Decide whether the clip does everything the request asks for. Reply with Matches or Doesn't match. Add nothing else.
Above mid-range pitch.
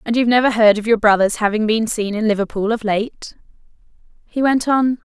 Matches